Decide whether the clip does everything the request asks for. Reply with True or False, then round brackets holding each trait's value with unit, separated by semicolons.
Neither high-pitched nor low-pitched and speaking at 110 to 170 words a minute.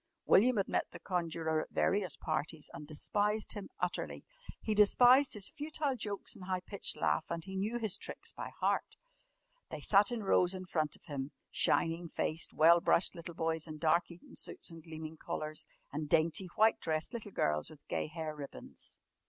False (170 Hz; 185 wpm)